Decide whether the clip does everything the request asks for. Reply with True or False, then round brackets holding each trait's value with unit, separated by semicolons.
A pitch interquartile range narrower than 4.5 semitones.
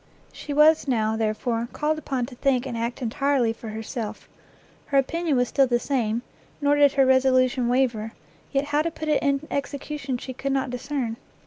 True (3.1 semitones)